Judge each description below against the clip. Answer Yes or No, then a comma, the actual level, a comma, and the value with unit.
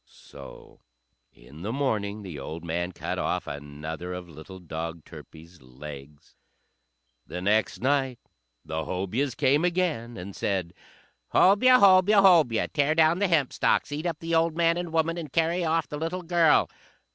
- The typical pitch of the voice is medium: No, low, 130 Hz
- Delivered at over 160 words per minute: No, average, 155 wpm